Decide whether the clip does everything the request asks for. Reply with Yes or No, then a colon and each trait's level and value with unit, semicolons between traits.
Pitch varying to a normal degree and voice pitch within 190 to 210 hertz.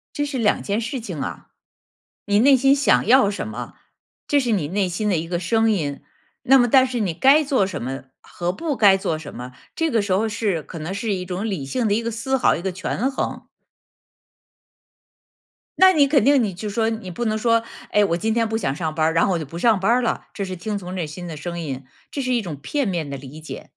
No: wide, 5.7 semitones; high, 205 Hz